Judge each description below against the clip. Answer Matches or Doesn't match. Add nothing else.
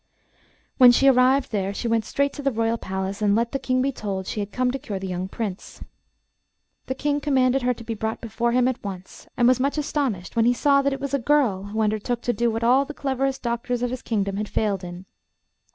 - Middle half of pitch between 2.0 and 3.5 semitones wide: Doesn't match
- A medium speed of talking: Doesn't match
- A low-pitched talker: Doesn't match